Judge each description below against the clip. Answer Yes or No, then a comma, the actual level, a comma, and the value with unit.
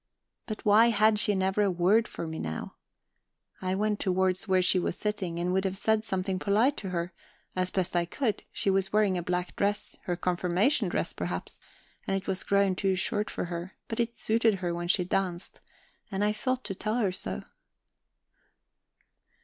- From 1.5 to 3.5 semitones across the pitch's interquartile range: Yes, average, 2.7 semitones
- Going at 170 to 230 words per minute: Yes, average, 190 wpm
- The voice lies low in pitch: No, high, 190 Hz